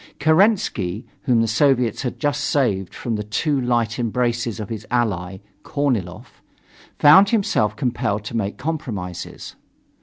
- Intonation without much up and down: No, average, 5.2 semitones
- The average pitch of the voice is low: Yes, low, 120 Hz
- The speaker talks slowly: Yes, slow, 130 wpm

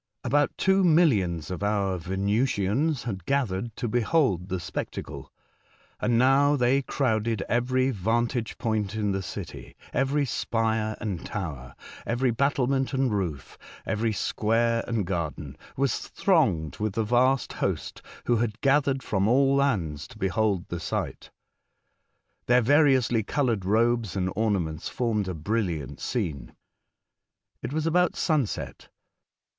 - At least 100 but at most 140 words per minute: Yes, slow, 135 wpm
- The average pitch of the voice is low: Yes, low, 115 Hz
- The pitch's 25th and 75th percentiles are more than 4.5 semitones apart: Yes, average, 5.3 semitones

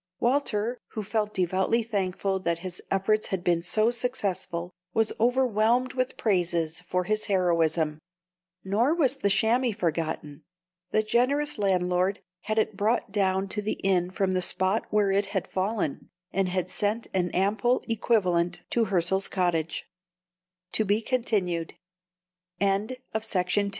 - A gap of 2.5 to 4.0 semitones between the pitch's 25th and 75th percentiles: Yes, average, 3.6 semitones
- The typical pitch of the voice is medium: No, high, 200 Hz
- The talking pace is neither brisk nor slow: No, slow, 115 wpm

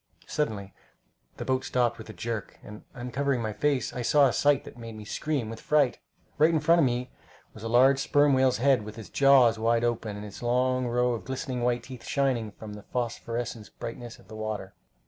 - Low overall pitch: Yes, low, 120 Hz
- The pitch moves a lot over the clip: No, average, 3.0 semitones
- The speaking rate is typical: No, fast, 210 wpm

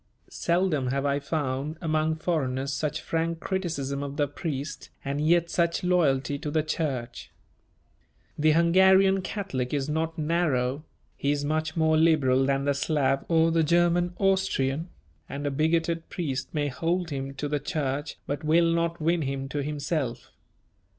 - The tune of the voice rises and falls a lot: No, average, 3.2 semitones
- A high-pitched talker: No, medium, 155 Hz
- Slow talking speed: No, average, 155 wpm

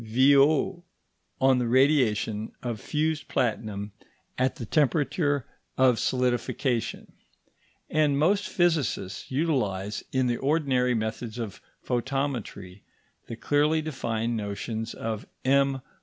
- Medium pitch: No, low, 130 Hz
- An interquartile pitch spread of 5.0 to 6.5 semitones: No, average, 4.3 semitones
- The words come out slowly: Yes, slow, 105 wpm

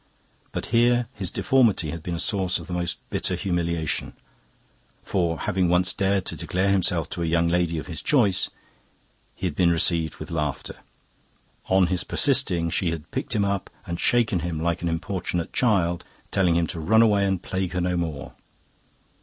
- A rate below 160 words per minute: No, average, 180 wpm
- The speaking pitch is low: Yes, very low, 90 Hz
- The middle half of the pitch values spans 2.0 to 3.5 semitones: Yes, narrow, 2.5 semitones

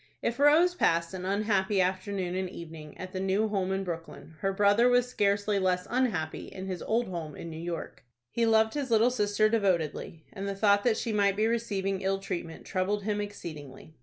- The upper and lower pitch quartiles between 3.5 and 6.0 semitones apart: No, average, 3.0 semitones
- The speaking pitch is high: Yes, high, 195 Hz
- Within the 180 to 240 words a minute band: Yes, average, 195 wpm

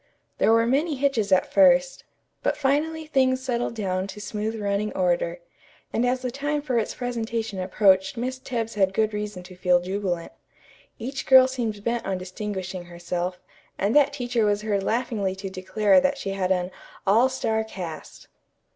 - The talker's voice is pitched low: No, high, 215 Hz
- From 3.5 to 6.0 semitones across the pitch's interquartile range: Yes, average, 5.2 semitones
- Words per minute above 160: Yes, average, 170 wpm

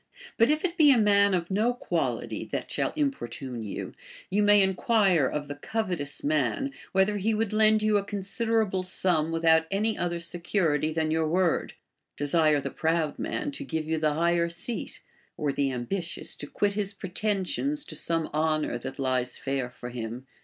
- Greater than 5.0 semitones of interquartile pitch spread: Yes, wide, 5.4 semitones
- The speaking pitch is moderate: Yes, medium, 175 Hz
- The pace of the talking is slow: No, average, 180 wpm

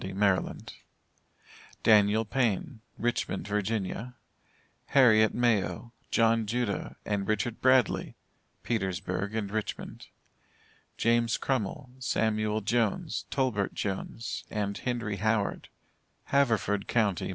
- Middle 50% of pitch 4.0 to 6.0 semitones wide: No, average, 2.9 semitones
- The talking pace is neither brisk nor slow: No, slow, 90 wpm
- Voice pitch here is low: Yes, low, 110 Hz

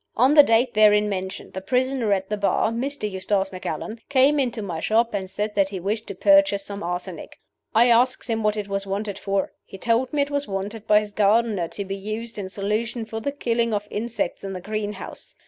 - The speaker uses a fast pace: Yes, fast, 215 wpm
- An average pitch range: Yes, average, 3.0 semitones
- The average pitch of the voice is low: No, high, 210 Hz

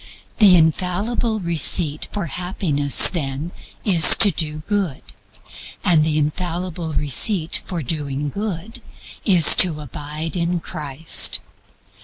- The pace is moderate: No, slow, 110 wpm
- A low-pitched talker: No, medium, 165 Hz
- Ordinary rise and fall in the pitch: Yes, average, 3.3 semitones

